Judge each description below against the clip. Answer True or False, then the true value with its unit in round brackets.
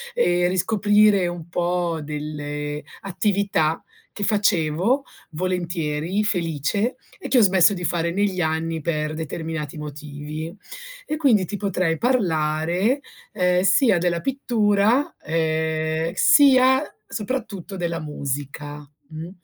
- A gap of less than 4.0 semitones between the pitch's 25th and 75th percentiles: False (4.5 semitones)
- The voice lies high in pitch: False (175 Hz)